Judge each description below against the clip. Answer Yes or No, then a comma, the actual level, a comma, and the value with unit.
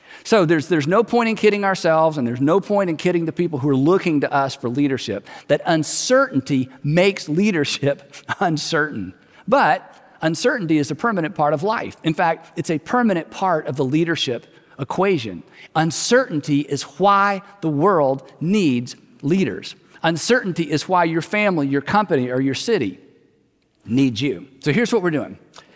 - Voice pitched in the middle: Yes, medium, 160 Hz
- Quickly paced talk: No, average, 165 wpm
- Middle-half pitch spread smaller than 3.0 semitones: No, average, 5.1 semitones